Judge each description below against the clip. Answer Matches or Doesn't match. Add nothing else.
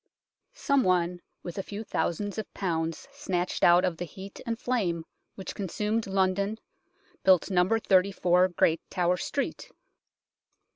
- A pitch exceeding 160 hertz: Matches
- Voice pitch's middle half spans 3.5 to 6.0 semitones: Doesn't match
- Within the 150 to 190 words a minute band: Doesn't match